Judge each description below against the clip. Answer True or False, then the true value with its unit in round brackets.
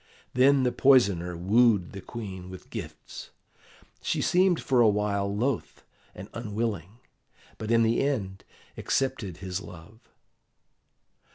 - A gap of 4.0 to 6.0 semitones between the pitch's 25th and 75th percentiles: True (4.4 semitones)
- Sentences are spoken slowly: True (120 wpm)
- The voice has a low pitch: True (105 Hz)